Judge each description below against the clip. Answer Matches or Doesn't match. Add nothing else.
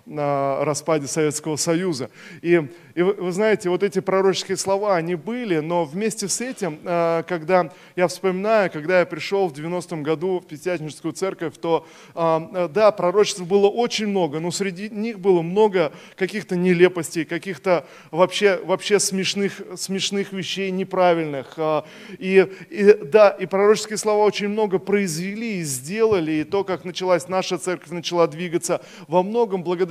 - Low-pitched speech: Doesn't match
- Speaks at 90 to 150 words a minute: Matches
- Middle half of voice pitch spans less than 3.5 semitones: Matches